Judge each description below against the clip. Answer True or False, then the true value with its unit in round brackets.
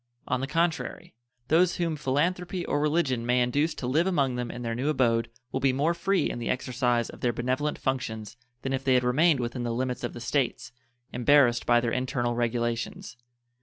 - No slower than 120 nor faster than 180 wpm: False (200 wpm)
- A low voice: True (130 Hz)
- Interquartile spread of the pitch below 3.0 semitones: False (3.9 semitones)